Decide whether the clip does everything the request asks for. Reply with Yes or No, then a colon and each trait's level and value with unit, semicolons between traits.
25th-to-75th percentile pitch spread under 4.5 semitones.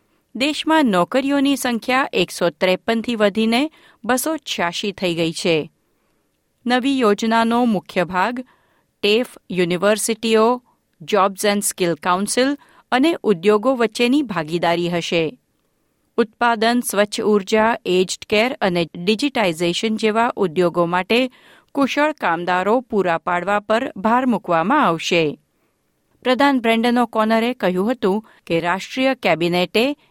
No: wide, 5.5 semitones